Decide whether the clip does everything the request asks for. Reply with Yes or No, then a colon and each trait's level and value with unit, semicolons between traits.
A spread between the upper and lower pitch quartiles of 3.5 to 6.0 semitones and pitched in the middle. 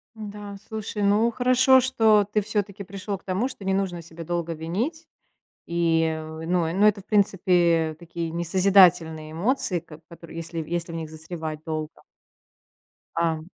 Yes: average, 3.9 semitones; medium, 175 Hz